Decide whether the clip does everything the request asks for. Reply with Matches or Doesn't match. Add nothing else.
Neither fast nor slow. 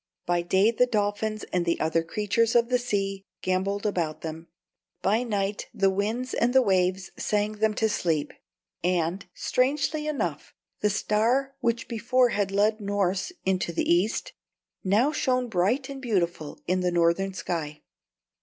Matches